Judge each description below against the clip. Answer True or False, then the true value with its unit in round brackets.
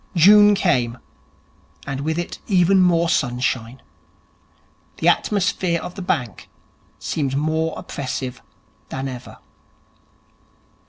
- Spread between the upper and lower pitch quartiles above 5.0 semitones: True (5.4 semitones)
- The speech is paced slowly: True (95 wpm)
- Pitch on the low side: False (155 Hz)